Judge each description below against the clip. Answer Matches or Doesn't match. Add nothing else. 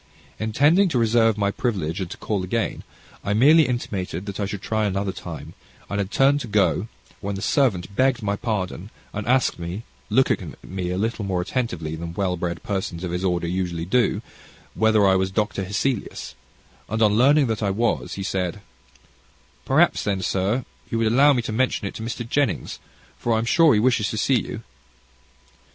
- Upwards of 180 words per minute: Matches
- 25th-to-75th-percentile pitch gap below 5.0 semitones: Matches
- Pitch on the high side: Doesn't match